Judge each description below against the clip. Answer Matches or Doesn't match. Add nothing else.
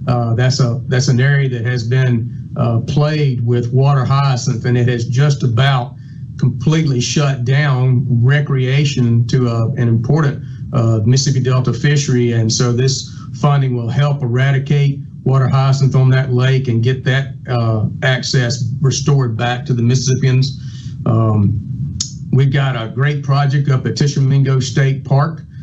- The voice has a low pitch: Matches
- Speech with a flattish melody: Matches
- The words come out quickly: Doesn't match